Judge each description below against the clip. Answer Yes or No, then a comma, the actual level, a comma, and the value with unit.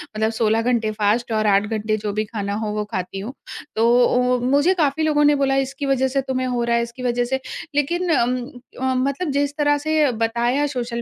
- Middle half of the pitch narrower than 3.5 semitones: No, average, 4.0 semitones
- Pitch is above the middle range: Yes, very high, 250 Hz